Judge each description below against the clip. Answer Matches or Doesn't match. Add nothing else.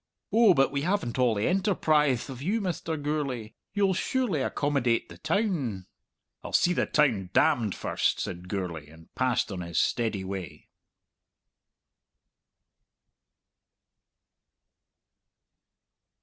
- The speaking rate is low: Matches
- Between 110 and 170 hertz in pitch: Matches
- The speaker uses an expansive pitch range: Matches